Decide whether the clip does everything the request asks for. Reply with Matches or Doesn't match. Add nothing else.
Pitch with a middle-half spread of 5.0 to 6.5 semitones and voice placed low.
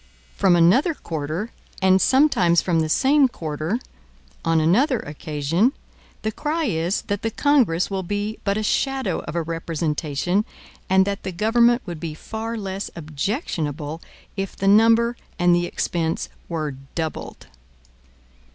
Doesn't match